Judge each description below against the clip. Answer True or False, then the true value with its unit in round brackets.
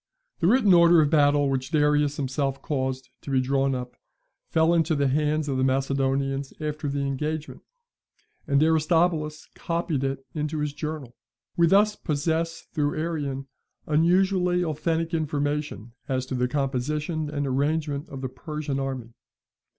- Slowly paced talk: False (145 wpm)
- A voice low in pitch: False (150 Hz)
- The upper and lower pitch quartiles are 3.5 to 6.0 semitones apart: False (2.8 semitones)